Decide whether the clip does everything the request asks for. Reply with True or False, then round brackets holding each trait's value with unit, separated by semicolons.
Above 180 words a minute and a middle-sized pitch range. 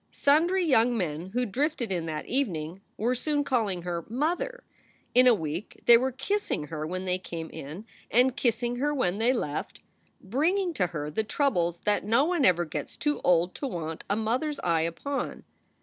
False (195 wpm; 8.3 semitones)